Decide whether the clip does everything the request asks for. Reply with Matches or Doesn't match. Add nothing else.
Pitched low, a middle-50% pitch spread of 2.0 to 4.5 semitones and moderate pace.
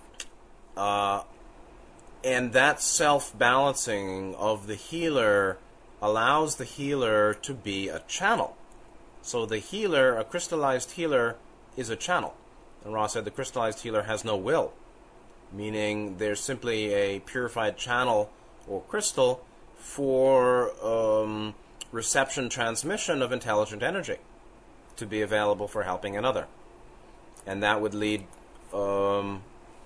Doesn't match